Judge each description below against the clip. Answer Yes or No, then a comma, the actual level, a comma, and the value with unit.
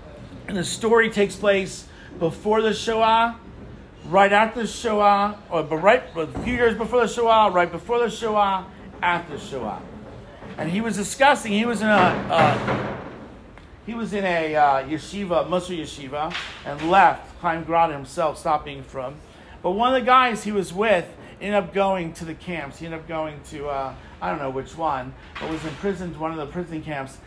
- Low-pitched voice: No, medium, 185 Hz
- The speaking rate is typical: Yes, average, 185 wpm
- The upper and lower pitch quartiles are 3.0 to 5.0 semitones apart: No, wide, 5.4 semitones